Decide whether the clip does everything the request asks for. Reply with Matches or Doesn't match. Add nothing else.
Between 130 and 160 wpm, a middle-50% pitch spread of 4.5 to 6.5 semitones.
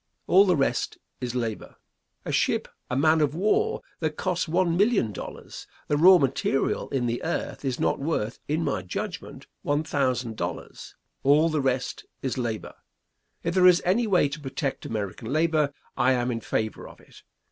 Doesn't match